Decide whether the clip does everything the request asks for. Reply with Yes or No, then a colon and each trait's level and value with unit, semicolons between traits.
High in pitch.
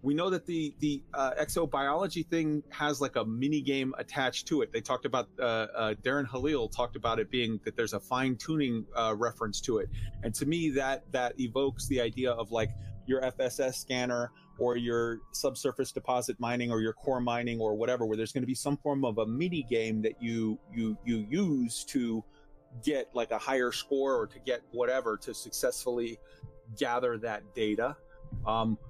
No: low, 125 Hz